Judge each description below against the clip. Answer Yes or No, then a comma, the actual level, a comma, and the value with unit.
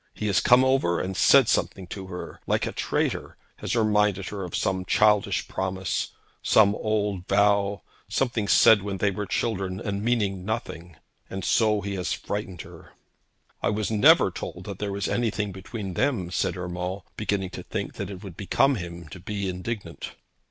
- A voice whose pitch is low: Yes, low, 100 Hz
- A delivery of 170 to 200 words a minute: Yes, average, 175 wpm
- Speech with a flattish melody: Yes, narrow, 2.3 semitones